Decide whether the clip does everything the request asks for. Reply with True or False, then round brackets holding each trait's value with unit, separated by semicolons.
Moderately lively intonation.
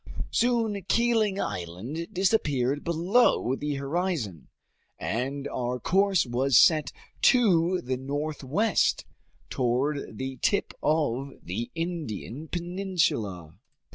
False (6.4 semitones)